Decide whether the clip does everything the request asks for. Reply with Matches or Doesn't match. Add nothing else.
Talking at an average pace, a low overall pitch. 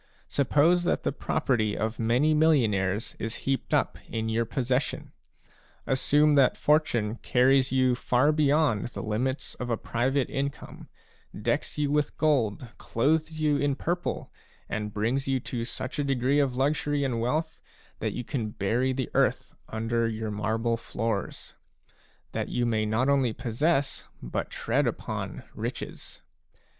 Matches